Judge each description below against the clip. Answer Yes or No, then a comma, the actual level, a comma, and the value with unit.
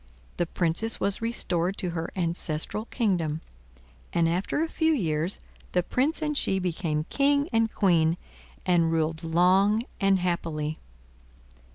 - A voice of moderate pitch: Yes, medium, 180 Hz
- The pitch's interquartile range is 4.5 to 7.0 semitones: Yes, average, 4.8 semitones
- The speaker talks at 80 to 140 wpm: Yes, slow, 135 wpm